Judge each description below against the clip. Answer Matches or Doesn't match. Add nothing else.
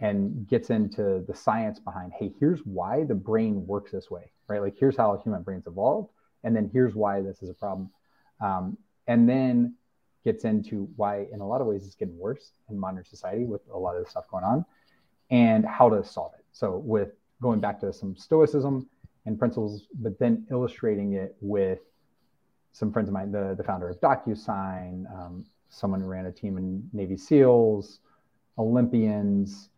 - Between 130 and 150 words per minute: Doesn't match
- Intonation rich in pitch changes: Doesn't match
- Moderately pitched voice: Doesn't match